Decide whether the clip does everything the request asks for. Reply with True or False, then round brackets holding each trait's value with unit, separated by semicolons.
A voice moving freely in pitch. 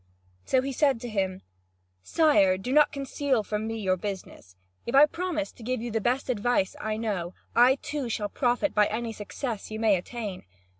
False (4.4 semitones)